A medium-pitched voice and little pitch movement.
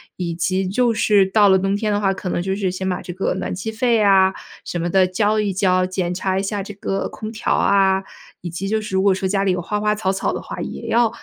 No: high, 195 Hz; narrow, 2.1 semitones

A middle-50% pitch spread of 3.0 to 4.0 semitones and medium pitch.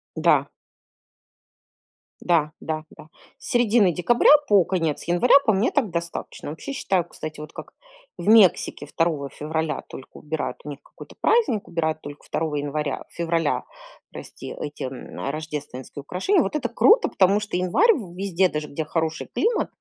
No: average, 4.8 semitones; medium, 170 Hz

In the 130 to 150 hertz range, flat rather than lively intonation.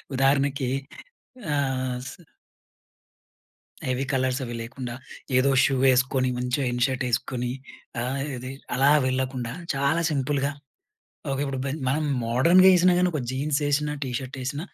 Yes: low, 135 Hz; narrow, 1.9 semitones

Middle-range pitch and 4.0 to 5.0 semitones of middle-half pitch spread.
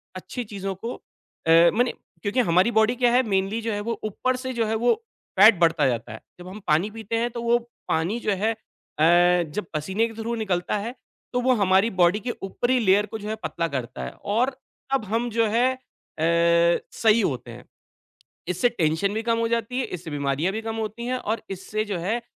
No: high, 210 Hz; average, 4.7 semitones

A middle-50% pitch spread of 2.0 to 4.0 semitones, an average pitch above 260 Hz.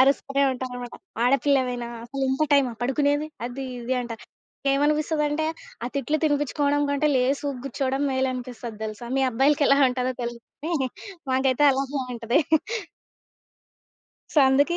Yes: narrow, 2.5 semitones; very high, 270 Hz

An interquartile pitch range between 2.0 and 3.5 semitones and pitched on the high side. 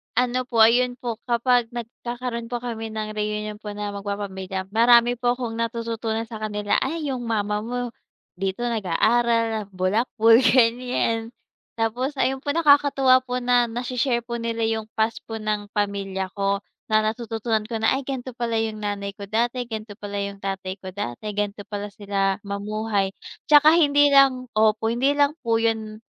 Yes: average, 2.8 semitones; high, 225 Hz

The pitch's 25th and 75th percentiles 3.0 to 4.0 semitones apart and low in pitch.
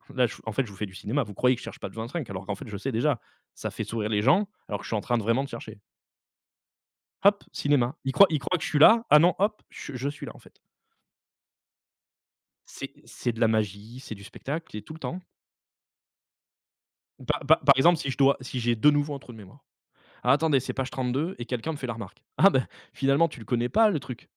No: average, 4.7 semitones; low, 130 Hz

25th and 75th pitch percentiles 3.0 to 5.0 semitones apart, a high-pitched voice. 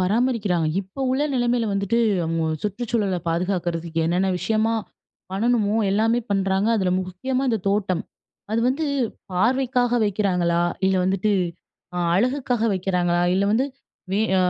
Yes: average, 4.3 semitones; high, 200 Hz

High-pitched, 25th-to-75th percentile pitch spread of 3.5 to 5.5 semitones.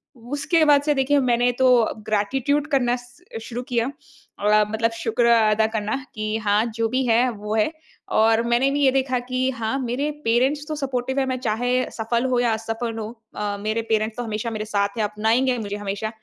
No: high, 235 Hz; average, 3.0 semitones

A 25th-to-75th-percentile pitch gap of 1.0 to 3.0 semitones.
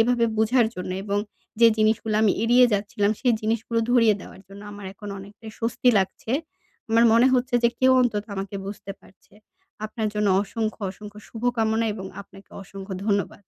Yes: narrow, 2.4 semitones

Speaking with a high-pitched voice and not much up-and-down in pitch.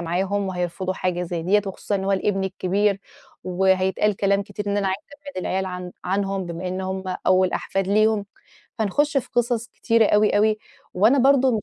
Yes: high, 195 Hz; narrow, 2.2 semitones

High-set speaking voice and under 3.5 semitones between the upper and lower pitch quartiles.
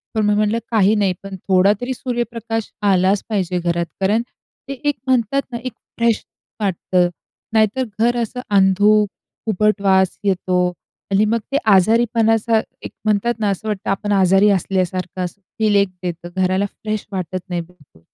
Yes: high, 205 Hz; average, 3.0 semitones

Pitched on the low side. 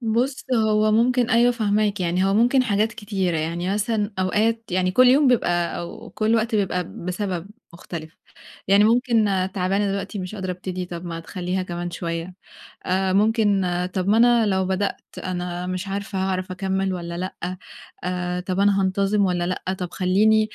No: high, 195 Hz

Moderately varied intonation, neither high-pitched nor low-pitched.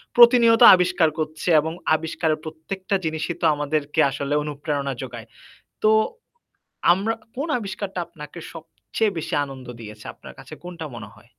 Yes: average, 4.5 semitones; medium, 160 Hz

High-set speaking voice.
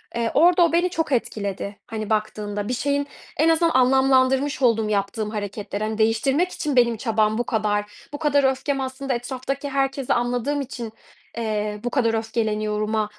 Yes: high, 240 Hz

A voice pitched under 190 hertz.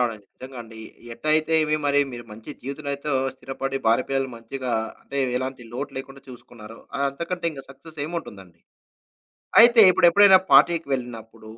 Yes: low, 135 Hz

